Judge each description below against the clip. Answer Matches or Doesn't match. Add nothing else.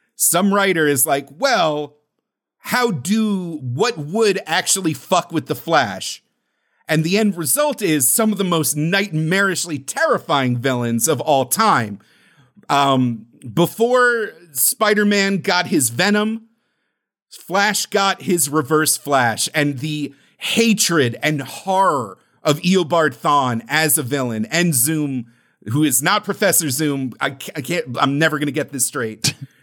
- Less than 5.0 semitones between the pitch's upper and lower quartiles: Doesn't match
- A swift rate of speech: Doesn't match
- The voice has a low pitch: Doesn't match